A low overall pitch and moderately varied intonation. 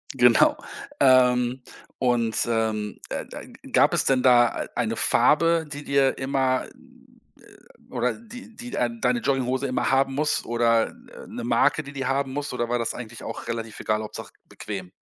Yes: low, 130 Hz; average, 3.2 semitones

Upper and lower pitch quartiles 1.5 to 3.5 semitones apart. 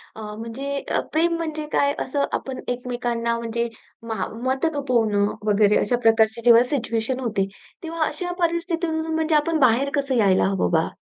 No: wide, 5.4 semitones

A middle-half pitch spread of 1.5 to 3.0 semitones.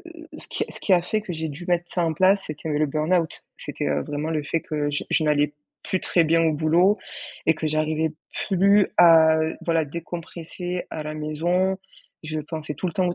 Yes: narrow, 2.6 semitones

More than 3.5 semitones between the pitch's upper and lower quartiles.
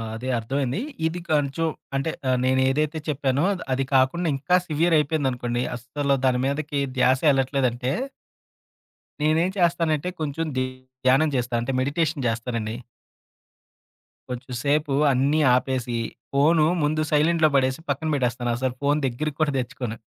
No: average, 3.2 semitones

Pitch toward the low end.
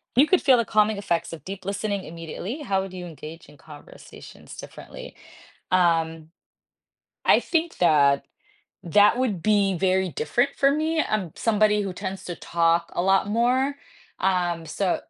No: high, 190 Hz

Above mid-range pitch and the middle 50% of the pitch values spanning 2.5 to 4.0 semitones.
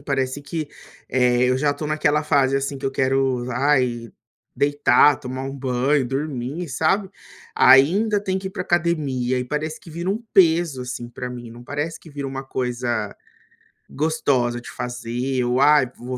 No: low, 135 Hz; average, 3.4 semitones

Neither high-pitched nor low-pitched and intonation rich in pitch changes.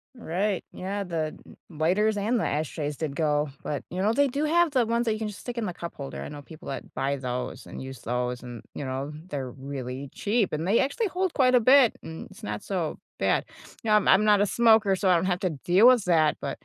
Yes: medium, 180 Hz; wide, 7.4 semitones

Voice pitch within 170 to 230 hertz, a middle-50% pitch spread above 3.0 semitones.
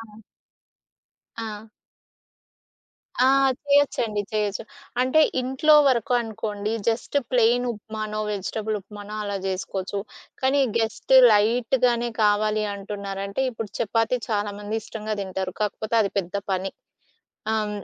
No: high, 215 Hz; narrow, 2.5 semitones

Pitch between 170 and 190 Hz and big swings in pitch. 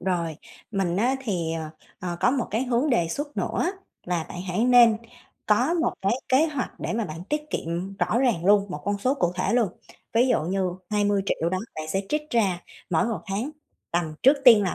No: high, 200 Hz; wide, 5.8 semitones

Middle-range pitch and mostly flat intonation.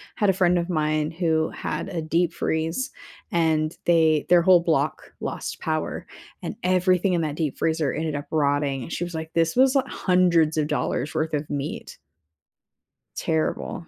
Yes: medium, 160 Hz; narrow, 2.3 semitones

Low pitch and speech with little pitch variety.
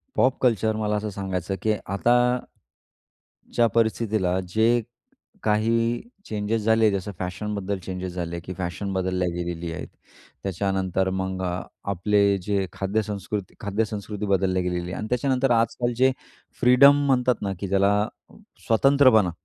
No: low, 105 Hz; average, 3.1 semitones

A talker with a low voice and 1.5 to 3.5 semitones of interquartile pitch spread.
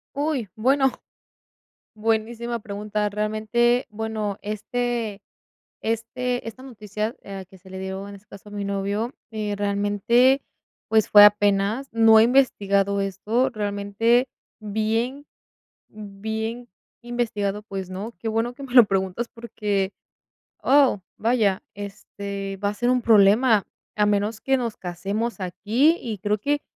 No: high, 215 Hz; average, 2.9 semitones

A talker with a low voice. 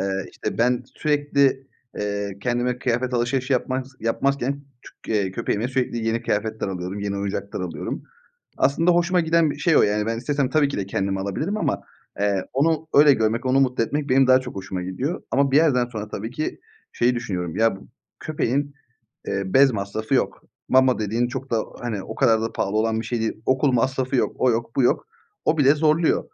Yes: low, 120 Hz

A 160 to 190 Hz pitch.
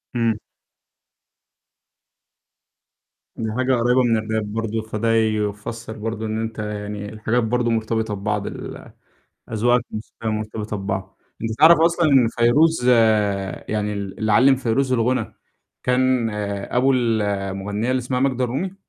No: low, 115 Hz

